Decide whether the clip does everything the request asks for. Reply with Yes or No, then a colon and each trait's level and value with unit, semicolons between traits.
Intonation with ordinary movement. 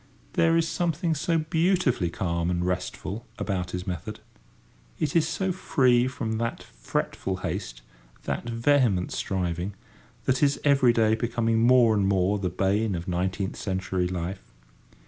No: wide, 6.4 semitones